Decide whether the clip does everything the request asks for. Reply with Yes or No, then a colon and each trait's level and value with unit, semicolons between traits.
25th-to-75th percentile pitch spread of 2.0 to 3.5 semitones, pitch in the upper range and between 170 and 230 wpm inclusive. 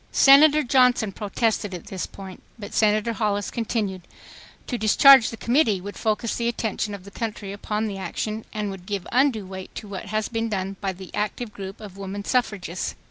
Yes: average, 2.7 semitones; high, 210 Hz; average, 190 wpm